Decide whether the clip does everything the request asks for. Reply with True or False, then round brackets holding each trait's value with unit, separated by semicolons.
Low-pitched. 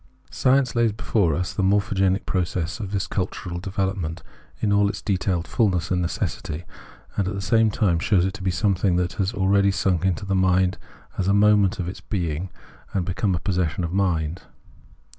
True (95 Hz)